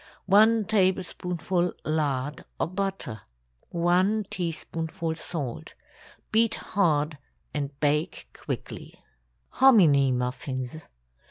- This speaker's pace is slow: Yes, slow, 80 wpm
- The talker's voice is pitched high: No, medium, 165 Hz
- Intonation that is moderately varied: Yes, average, 4.7 semitones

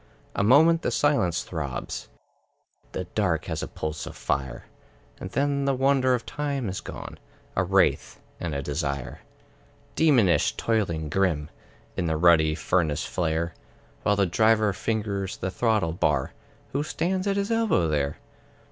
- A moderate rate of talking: Yes, average, 145 wpm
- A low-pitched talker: Yes, very low, 95 Hz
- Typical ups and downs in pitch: No, wide, 8.7 semitones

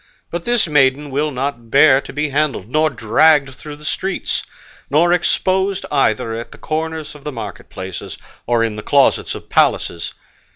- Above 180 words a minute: No, average, 170 wpm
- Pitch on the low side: No, medium, 145 Hz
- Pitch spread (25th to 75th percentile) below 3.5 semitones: No, average, 4.6 semitones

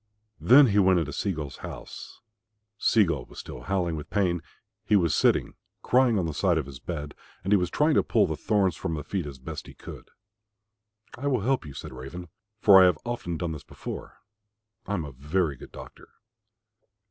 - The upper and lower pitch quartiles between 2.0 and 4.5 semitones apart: No, average, 5.3 semitones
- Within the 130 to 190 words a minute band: No, fast, 205 wpm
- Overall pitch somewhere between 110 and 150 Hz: No, very low, 90 Hz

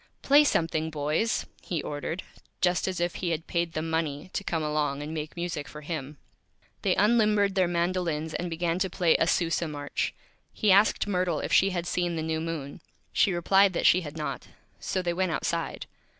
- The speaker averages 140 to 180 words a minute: No, average, 195 wpm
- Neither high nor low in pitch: Yes, medium, 170 Hz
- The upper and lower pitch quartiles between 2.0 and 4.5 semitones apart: Yes, average, 2.8 semitones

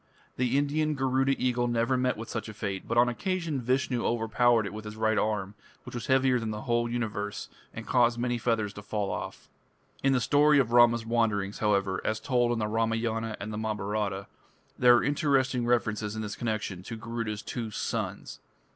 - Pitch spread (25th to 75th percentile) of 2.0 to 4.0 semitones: Yes, average, 2.7 semitones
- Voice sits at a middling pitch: No, low, 115 Hz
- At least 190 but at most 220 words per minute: Yes, average, 195 wpm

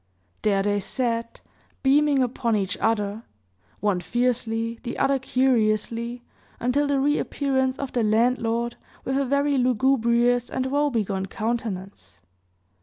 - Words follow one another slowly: Yes, slow, 120 wpm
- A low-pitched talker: No, high, 240 Hz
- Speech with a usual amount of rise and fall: Yes, average, 3.2 semitones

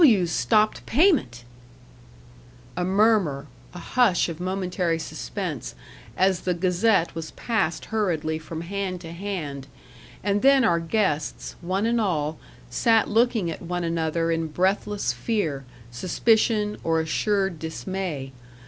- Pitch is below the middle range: No, medium, 180 Hz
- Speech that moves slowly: Yes, slow, 130 wpm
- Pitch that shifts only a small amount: No, average, 4.3 semitones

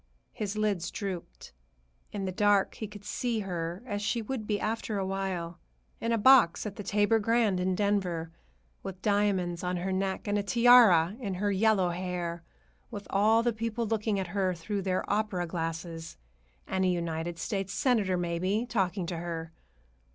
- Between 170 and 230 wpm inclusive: Yes, average, 175 wpm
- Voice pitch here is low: No, high, 195 Hz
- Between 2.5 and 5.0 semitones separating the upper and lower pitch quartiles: Yes, average, 3.2 semitones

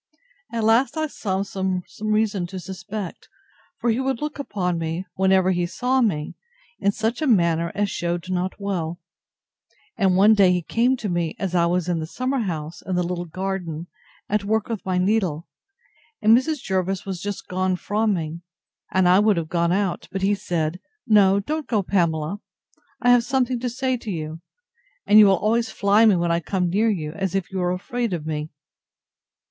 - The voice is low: No, high, 190 Hz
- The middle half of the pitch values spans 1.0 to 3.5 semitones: No, average, 3.9 semitones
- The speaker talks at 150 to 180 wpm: No, average, 190 wpm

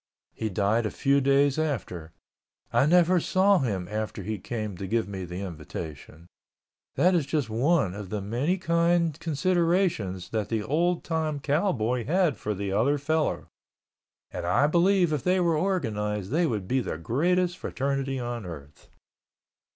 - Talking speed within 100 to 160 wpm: Yes, average, 155 wpm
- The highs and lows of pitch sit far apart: Yes, wide, 8.2 semitones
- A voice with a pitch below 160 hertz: Yes, low, 135 Hz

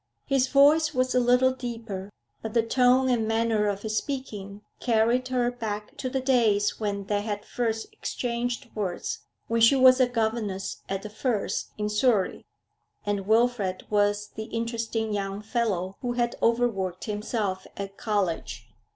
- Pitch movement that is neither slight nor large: Yes, average, 3.1 semitones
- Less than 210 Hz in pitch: No, high, 225 Hz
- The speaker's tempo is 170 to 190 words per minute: No, average, 155 wpm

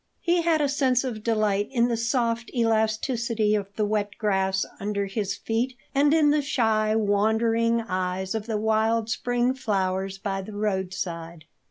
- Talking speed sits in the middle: Yes, average, 160 wpm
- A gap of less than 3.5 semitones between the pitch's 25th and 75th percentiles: Yes, average, 2.8 semitones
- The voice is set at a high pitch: Yes, high, 220 Hz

